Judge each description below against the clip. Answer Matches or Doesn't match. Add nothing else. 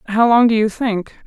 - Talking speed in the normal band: Doesn't match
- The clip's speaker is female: Matches